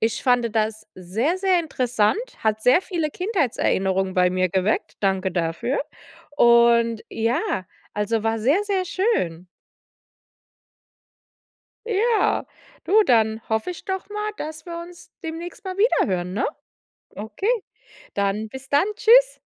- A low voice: No, high, 235 Hz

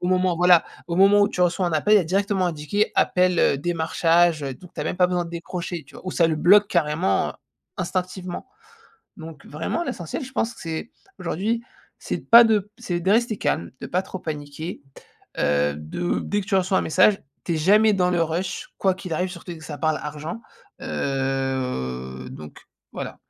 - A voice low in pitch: No, medium, 175 Hz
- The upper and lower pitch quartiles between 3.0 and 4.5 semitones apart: Yes, average, 3.4 semitones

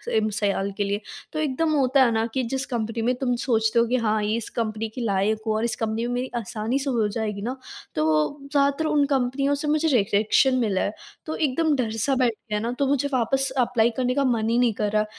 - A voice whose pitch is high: Yes, high, 235 Hz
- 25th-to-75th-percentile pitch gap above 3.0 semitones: Yes, average, 3.6 semitones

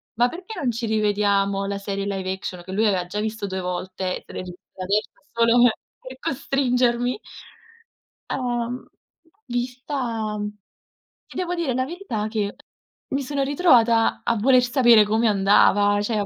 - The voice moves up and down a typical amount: Yes, average, 3.9 semitones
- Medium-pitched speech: No, high, 225 Hz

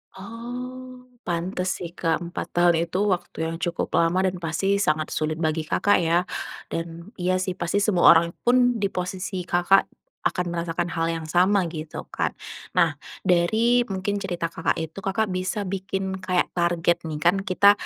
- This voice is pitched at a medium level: Yes, medium, 180 Hz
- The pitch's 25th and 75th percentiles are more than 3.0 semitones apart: No, average, 2.7 semitones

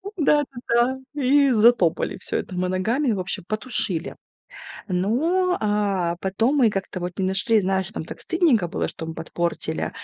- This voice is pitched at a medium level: No, high, 210 Hz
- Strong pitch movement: Yes, wide, 5.9 semitones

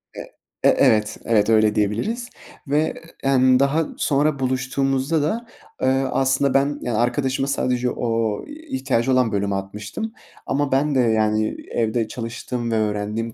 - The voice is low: Yes, low, 125 Hz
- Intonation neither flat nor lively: Yes, average, 3.9 semitones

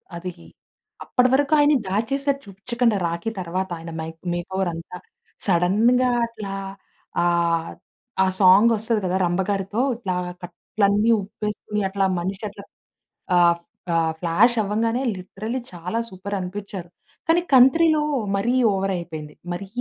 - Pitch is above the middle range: Yes, high, 195 Hz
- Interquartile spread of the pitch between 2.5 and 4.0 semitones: No, average, 4.6 semitones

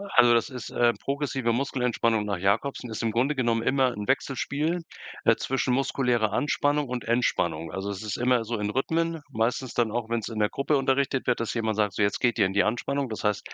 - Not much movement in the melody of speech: No, average, 3.6 semitones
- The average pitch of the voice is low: Yes, low, 120 Hz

